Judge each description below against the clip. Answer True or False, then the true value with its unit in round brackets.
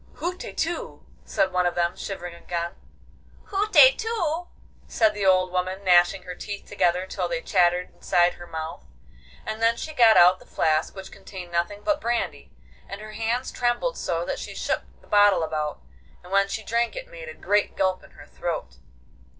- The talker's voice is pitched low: False (195 Hz)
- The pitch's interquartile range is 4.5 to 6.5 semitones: True (5.1 semitones)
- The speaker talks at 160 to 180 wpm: True (175 wpm)